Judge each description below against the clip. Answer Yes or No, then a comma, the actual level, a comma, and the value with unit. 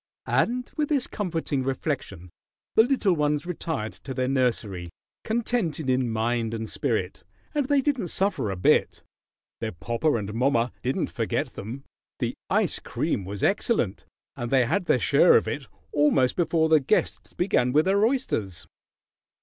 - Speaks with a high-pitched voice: No, low, 135 Hz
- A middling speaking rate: Yes, average, 155 wpm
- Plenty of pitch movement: Yes, wide, 8.4 semitones